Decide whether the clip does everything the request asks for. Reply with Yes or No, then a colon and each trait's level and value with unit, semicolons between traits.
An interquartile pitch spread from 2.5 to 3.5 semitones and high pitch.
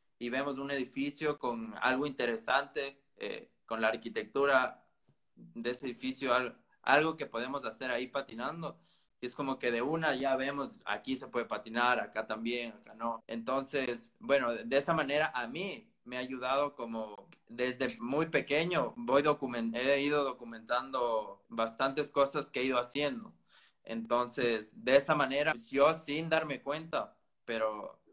No: average, 3.2 semitones; low, 130 Hz